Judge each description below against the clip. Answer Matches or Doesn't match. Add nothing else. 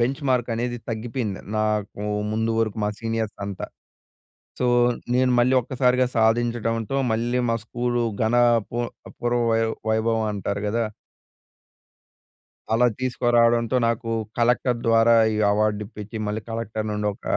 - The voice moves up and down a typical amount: Doesn't match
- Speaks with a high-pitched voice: Doesn't match